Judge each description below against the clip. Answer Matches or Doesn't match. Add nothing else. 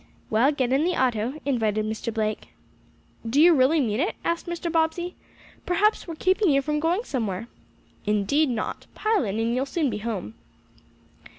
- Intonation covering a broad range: Matches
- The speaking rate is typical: Matches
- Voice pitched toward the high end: Matches